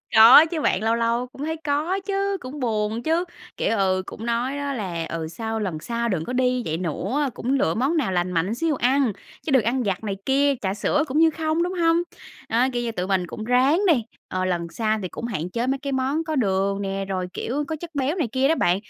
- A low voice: No, high, 240 Hz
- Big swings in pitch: Yes, wide, 6.5 semitones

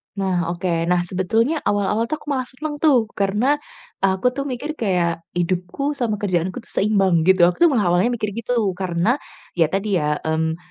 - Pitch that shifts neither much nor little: No, wide, 5.7 semitones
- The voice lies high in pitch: Yes, high, 195 Hz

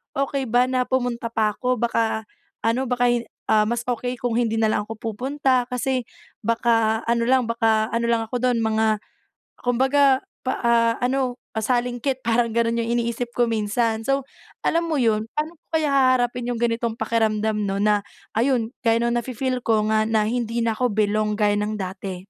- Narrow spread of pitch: Yes, narrow, 2.1 semitones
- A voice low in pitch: No, high, 235 Hz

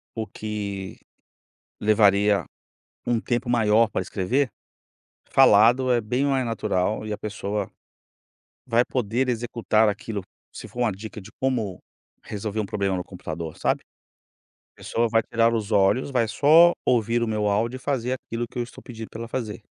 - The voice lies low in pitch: Yes, low, 110 Hz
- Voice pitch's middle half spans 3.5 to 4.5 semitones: No, average, 2.7 semitones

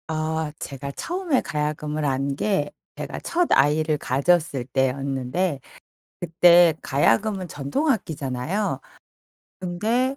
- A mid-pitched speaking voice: Yes, medium, 155 Hz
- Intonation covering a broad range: No, average, 5.0 semitones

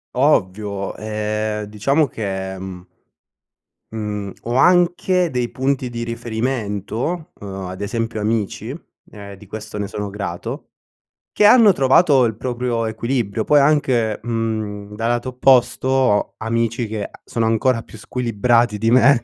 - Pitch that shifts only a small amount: No, average, 3.4 semitones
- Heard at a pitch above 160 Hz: No, low, 115 Hz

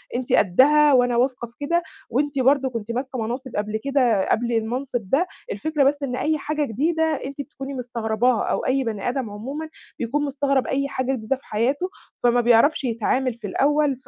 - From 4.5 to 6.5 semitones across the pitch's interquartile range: No, average, 3.3 semitones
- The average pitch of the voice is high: Yes, very high, 260 Hz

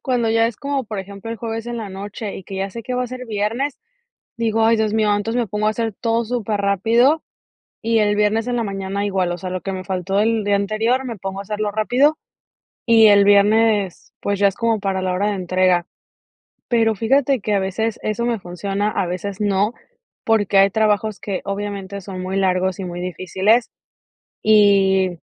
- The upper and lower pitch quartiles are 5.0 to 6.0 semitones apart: No, average, 2.7 semitones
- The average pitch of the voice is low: No, high, 205 Hz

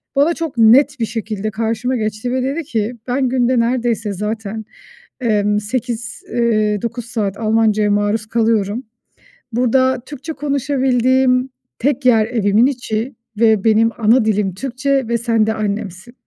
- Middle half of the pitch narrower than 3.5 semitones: Yes, average, 3.0 semitones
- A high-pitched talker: Yes, high, 230 Hz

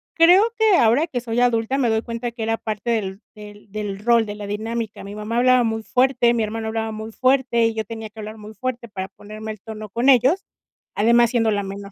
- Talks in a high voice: Yes, high, 225 Hz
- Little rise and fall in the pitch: Yes, narrow, 2.1 semitones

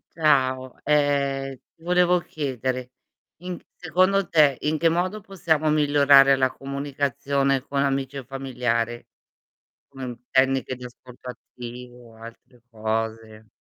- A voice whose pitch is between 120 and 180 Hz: Yes, low, 135 Hz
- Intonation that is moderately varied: Yes, average, 3.1 semitones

